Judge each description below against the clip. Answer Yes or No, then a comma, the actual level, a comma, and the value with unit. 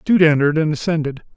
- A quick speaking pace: No, average, 175 wpm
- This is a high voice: No, medium, 155 Hz